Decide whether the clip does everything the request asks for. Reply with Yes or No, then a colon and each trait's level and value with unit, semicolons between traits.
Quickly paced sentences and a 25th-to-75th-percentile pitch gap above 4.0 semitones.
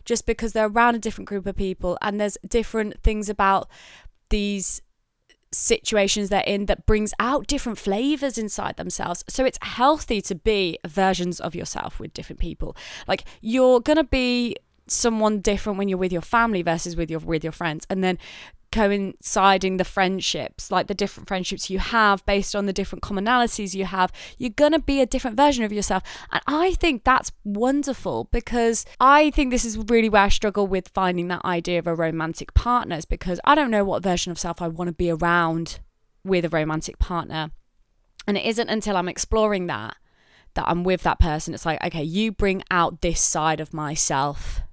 No: average, 190 wpm; average, 4.6 semitones